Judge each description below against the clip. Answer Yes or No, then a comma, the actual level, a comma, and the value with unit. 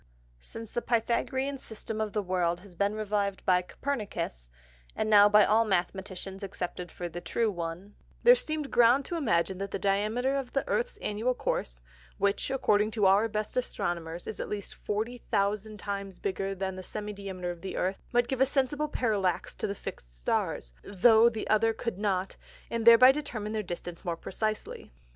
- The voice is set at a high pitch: Yes, high, 210 Hz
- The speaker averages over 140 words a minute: Yes, average, 180 wpm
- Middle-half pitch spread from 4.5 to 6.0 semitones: No, average, 3.5 semitones